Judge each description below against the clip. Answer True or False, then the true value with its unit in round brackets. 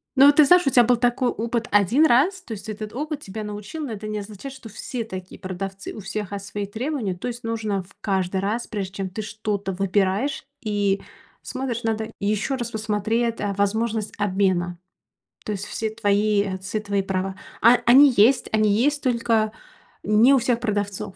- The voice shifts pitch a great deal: False (3.2 semitones)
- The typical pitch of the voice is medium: False (215 Hz)